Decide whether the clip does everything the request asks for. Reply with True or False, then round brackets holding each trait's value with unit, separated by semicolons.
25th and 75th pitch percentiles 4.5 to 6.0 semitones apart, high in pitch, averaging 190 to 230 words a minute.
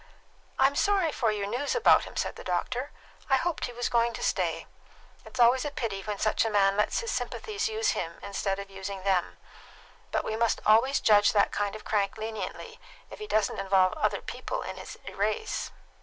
True (5.3 semitones; 220 Hz; 200 wpm)